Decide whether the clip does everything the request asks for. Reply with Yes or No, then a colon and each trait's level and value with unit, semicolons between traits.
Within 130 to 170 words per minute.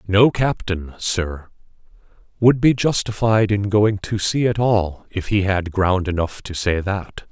Yes: average, 165 wpm